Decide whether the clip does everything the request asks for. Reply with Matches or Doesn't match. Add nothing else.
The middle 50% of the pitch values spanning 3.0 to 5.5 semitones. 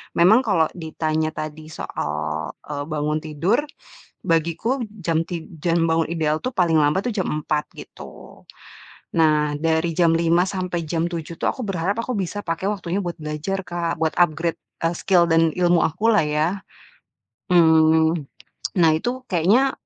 Doesn't match